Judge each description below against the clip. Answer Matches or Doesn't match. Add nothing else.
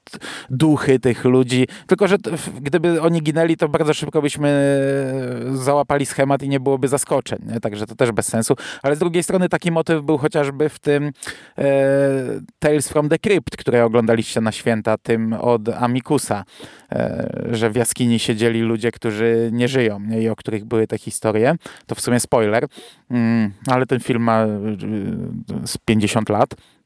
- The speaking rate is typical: Doesn't match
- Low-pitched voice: Matches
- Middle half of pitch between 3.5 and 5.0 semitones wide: Matches